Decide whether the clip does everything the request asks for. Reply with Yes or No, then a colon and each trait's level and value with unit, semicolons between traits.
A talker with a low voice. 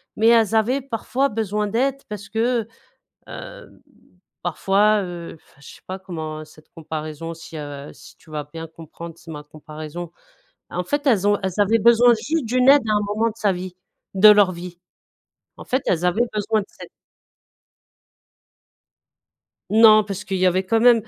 No: high, 205 Hz